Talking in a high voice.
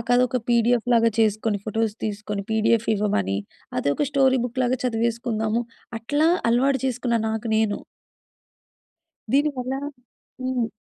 Yes: high, 230 Hz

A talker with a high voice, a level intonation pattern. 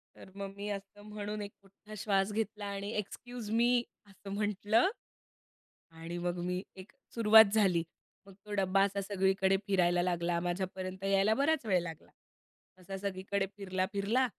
Yes: high, 195 Hz; narrow, 2.0 semitones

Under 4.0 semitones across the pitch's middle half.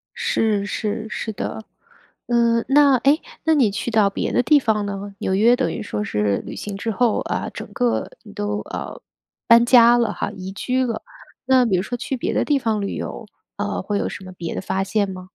Yes: average, 3.5 semitones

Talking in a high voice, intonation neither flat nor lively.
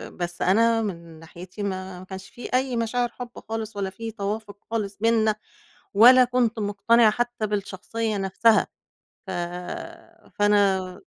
Yes: high, 210 Hz; average, 3.1 semitones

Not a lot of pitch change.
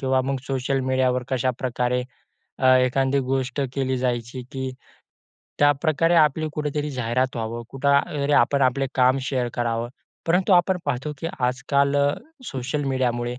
Yes: narrow, 2.1 semitones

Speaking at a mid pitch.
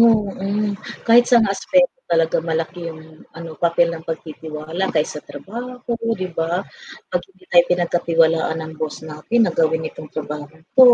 Yes: medium, 165 Hz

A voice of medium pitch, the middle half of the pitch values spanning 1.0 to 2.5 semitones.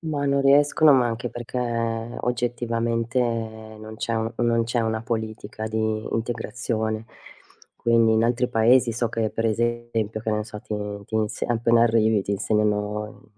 No: low, 115 Hz; narrow, 1.4 semitones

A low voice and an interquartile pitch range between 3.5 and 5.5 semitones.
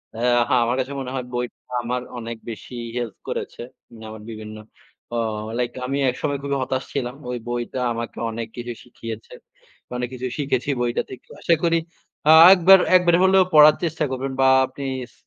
No: low, 125 Hz; average, 3.0 semitones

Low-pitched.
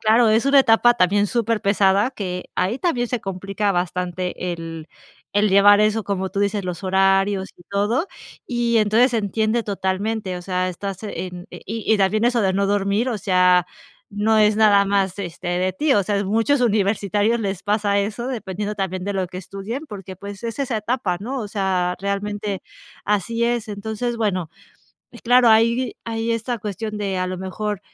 No: high, 205 Hz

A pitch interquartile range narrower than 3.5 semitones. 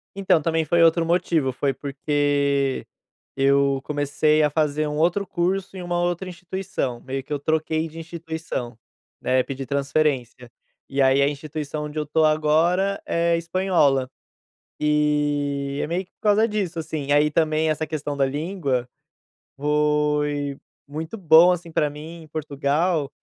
Yes: average, 2.9 semitones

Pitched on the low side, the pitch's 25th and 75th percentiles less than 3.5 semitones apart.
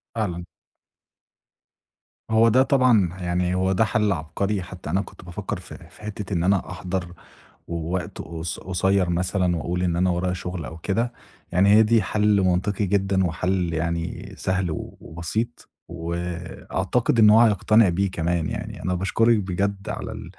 Yes: very low, 95 Hz; average, 2.9 semitones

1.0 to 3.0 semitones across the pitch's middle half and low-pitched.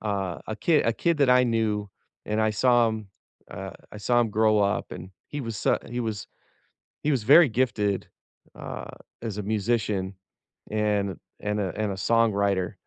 Yes: narrow, 2.6 semitones; low, 110 Hz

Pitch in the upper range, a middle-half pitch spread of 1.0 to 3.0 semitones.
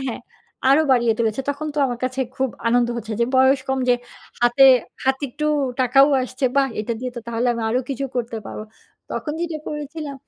Yes: very high, 260 Hz; narrow, 2.6 semitones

